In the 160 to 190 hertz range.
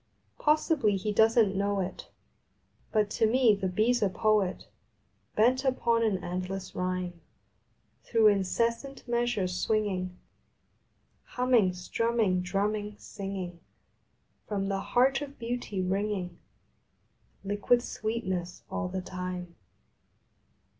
No: high, 205 Hz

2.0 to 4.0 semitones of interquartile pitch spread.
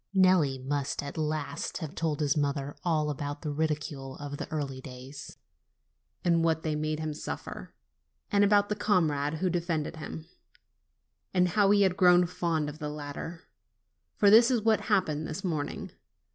Yes: average, 3.7 semitones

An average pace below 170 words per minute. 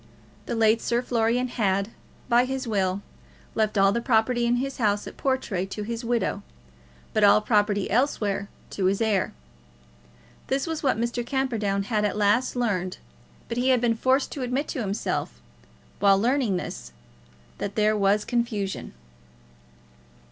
Yes: average, 155 wpm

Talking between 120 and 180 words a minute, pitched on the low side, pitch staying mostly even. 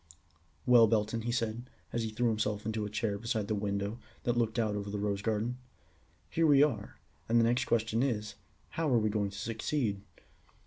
No: average, 195 wpm; low, 110 Hz; narrow, 2.3 semitones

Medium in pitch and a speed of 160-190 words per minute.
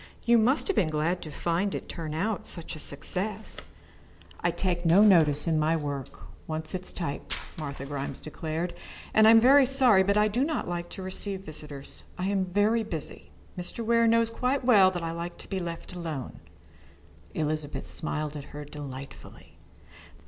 Yes: medium, 175 Hz; average, 185 wpm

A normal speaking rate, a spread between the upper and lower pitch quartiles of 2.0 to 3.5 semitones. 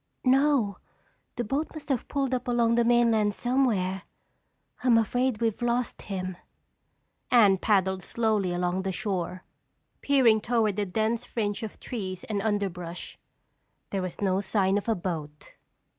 No: average, 145 wpm; average, 4.1 semitones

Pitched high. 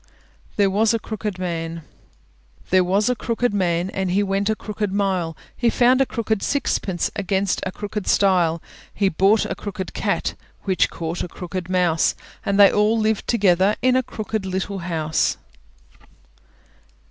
Yes: high, 195 Hz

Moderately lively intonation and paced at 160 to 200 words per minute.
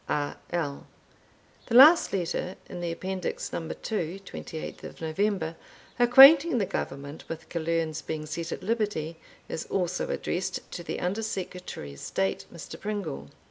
No: average, 4.3 semitones; average, 140 wpm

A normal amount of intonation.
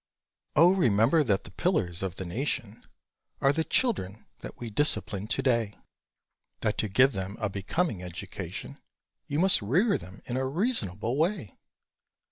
No: wide, 7.8 semitones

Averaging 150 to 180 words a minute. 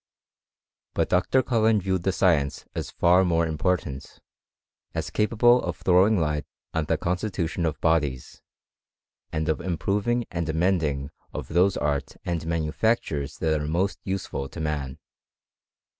No: slow, 135 wpm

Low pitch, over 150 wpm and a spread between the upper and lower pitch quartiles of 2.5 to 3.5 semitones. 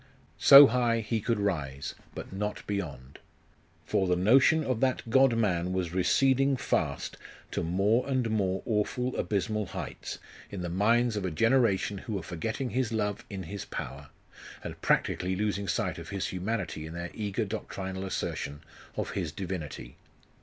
No: low, 100 Hz; average, 160 wpm; average, 4.2 semitones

